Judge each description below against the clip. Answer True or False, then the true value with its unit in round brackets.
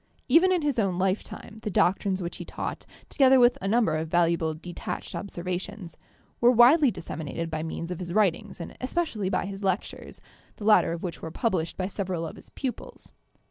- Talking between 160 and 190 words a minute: True (185 wpm)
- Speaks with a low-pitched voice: False (190 Hz)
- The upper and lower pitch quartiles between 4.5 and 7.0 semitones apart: True (5.2 semitones)